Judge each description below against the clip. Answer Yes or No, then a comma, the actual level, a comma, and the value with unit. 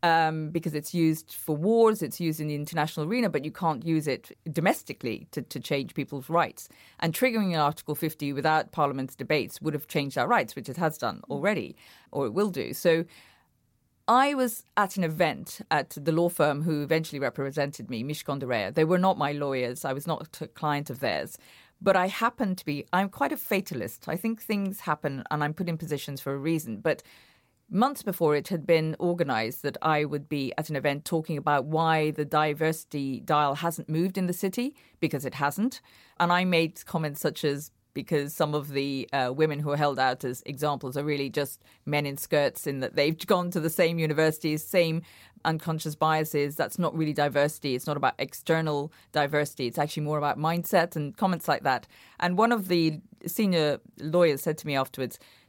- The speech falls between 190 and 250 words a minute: Yes, average, 200 wpm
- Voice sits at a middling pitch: Yes, medium, 155 Hz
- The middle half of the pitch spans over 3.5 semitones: No, average, 2.9 semitones